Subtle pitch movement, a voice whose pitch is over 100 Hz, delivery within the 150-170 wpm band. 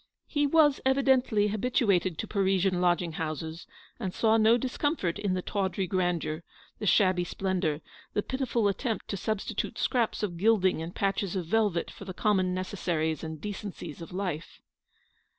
No: average, 3.7 semitones; high, 190 Hz; average, 155 wpm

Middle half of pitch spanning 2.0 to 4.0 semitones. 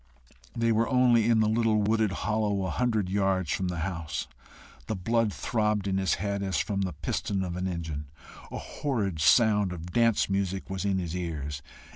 Yes: average, 3.3 semitones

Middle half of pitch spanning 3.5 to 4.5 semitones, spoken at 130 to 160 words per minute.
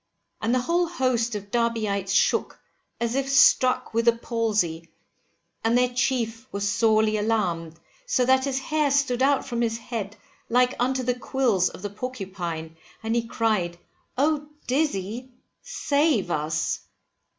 Yes: average, 4.2 semitones; average, 145 wpm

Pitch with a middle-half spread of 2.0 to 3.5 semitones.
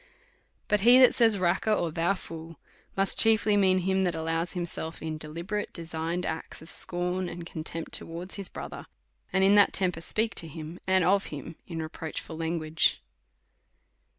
Yes: average, 2.9 semitones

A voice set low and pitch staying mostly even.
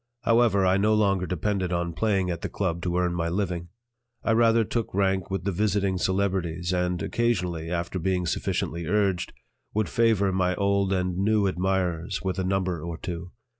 Yes: very low, 95 Hz; narrow, 2.2 semitones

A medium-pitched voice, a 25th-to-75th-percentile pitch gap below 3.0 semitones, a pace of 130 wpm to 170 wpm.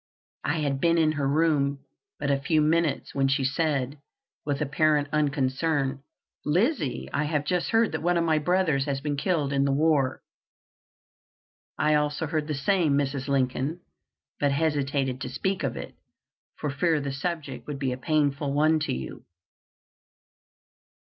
Yes: medium, 145 Hz; narrow, 2.5 semitones; average, 160 wpm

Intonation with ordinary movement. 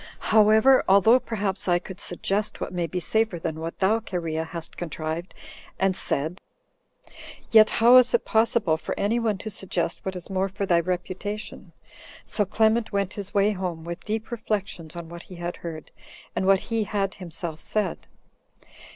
Yes: average, 3.8 semitones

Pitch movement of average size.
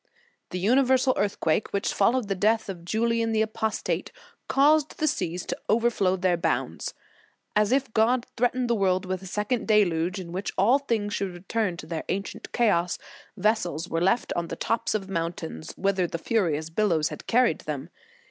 Yes: average, 4.4 semitones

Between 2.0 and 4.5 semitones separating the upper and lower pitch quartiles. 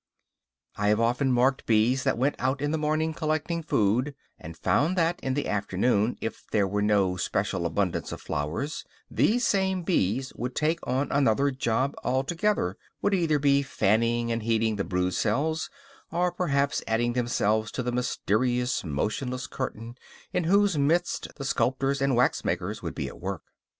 No: wide, 5.4 semitones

